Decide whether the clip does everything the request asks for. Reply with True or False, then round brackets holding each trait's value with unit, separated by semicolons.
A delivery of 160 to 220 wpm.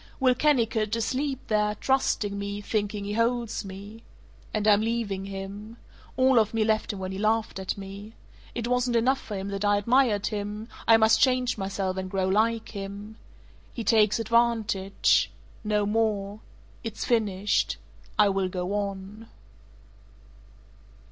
False (150 wpm)